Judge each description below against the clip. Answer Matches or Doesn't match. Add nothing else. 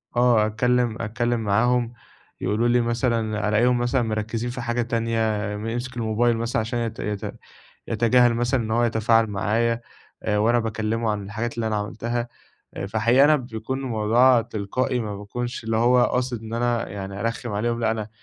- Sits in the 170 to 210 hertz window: Doesn't match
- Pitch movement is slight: Matches